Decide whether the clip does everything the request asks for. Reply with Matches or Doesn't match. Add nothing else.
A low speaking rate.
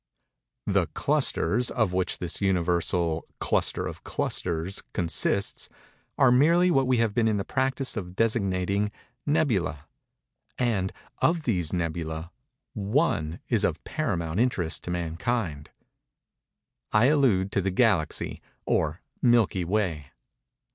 Matches